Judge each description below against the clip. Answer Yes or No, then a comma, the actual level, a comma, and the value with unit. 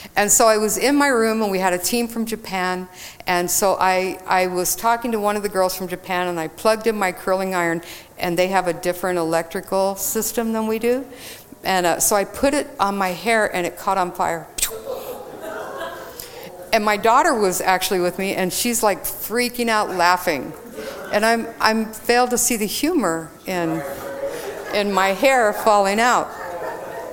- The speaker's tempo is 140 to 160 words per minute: No, average, 190 wpm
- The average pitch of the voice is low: No, high, 195 Hz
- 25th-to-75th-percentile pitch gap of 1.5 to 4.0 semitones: Yes, average, 3.7 semitones